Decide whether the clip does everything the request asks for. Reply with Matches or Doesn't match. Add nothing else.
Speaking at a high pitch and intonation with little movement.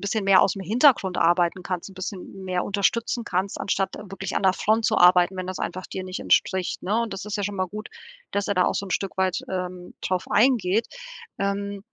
Matches